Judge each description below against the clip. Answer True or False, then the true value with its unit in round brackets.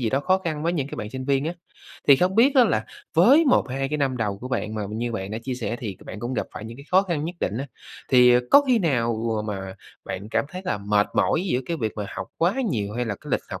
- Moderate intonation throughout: False (7.4 semitones)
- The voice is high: False (125 Hz)